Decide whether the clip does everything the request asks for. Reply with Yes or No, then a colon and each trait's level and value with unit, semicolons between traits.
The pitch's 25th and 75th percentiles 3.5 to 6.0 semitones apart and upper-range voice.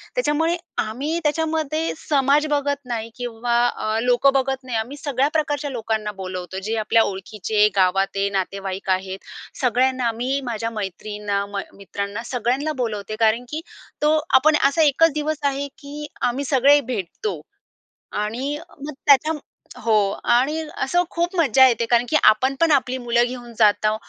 Yes: average, 4.9 semitones; high, 245 Hz